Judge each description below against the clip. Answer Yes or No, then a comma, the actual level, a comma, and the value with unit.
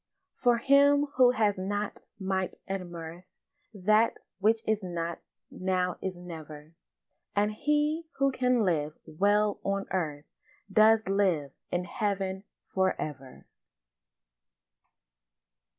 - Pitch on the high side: Yes, high, 195 Hz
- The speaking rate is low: Yes, slow, 110 wpm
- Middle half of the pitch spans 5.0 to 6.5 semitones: No, average, 3.9 semitones